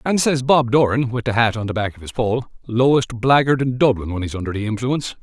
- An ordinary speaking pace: No, fast, 255 wpm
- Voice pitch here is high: No, low, 120 Hz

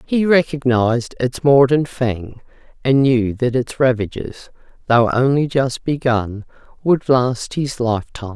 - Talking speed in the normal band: No, slow, 130 wpm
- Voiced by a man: No, female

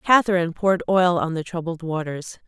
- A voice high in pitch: No, medium, 175 Hz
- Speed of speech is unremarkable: Yes, average, 170 wpm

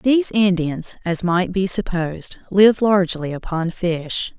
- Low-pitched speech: No, medium, 185 Hz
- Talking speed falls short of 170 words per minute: Yes, slow, 135 wpm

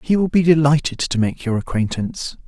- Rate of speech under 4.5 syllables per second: No, 5.7 syllables/s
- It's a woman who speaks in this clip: No, male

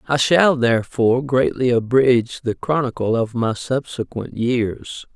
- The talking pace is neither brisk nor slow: No, slow, 130 wpm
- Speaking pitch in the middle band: No, low, 125 Hz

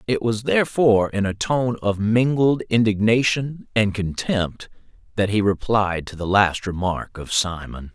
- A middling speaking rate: Yes, average, 150 wpm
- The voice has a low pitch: Yes, low, 105 Hz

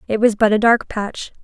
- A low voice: No, high, 220 Hz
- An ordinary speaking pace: No, fast, 250 wpm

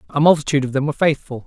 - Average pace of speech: No, fast, 245 wpm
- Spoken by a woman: No, male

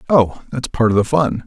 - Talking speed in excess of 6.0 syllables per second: No, 5.3 syllables/s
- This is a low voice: Yes, low, 125 Hz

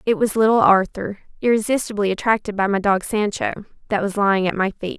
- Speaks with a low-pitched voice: No, high, 205 Hz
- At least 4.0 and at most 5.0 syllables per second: No, 6.0 syllables/s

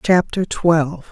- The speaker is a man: No, female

